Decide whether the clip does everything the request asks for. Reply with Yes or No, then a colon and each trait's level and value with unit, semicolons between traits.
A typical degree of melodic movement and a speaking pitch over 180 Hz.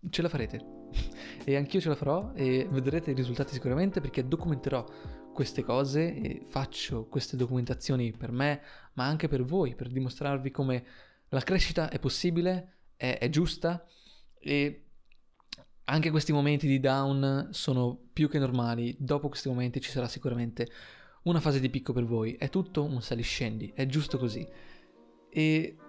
No: average, 3.4 semitones; low, 135 Hz